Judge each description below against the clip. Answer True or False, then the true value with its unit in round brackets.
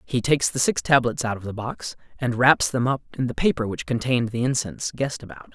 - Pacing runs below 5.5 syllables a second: False (6.2 syllables/s)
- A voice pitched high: False (120 Hz)